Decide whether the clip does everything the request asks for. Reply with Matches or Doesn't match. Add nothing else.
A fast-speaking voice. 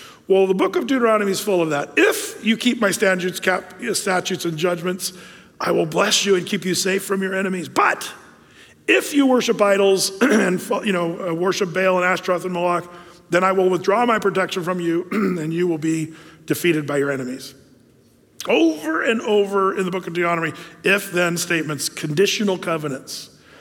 Doesn't match